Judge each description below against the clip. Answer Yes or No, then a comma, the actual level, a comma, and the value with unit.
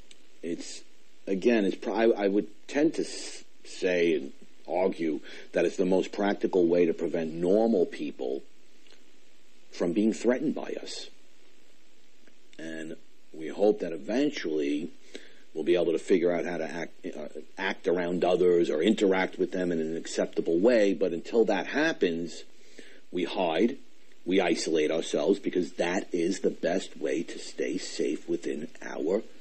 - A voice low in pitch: Yes, very low, 90 Hz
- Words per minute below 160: Yes, average, 145 wpm